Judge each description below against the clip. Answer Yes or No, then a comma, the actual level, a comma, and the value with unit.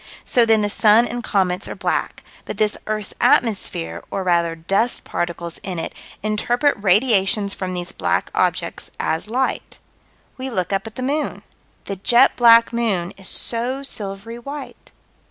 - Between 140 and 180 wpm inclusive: Yes, average, 155 wpm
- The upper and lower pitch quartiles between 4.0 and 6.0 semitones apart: Yes, average, 4.3 semitones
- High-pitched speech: Yes, high, 210 Hz